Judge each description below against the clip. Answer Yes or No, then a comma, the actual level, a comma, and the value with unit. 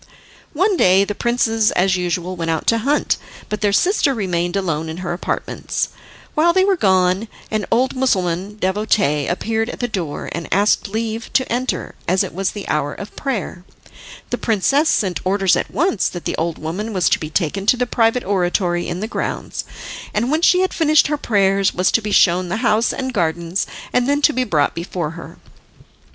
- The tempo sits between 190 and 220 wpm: Yes, average, 195 wpm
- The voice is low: No, high, 200 Hz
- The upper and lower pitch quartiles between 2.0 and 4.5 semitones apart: No, average, 5.3 semitones